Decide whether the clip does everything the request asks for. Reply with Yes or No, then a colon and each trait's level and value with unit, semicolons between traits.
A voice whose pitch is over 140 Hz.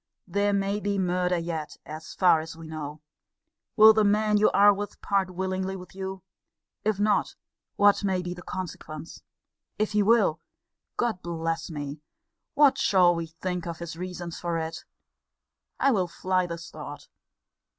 Yes: medium, 185 Hz